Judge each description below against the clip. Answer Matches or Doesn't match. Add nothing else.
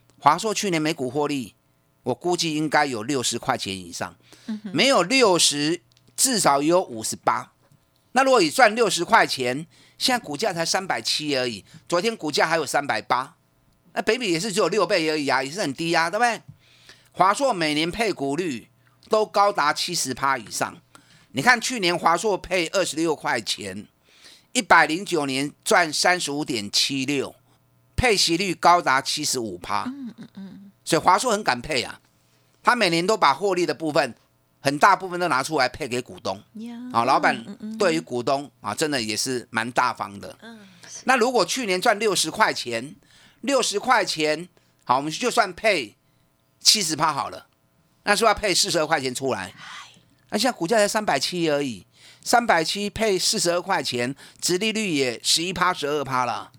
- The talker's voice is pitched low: Doesn't match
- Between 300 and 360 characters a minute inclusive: Doesn't match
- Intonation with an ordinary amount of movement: Doesn't match